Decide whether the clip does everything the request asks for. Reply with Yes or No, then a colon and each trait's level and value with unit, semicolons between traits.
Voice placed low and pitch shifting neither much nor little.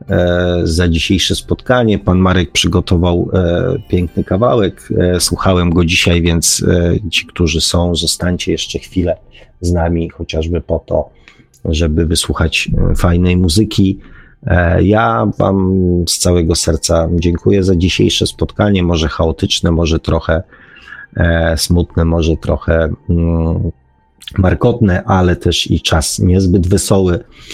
No: very low, 90 Hz; narrow, 2.0 semitones